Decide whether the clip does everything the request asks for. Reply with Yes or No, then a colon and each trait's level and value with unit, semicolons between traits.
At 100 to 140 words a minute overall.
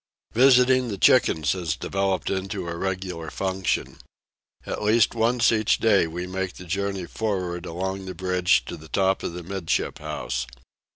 No: average, 160 wpm